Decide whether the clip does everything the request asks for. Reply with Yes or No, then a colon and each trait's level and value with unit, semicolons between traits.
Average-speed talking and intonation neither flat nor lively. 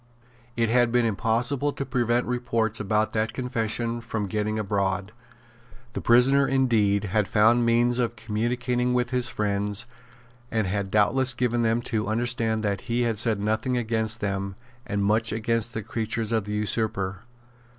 No: average, 155 wpm; narrow, 2.3 semitones